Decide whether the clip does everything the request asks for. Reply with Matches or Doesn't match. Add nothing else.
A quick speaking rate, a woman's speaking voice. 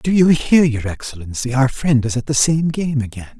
Doesn't match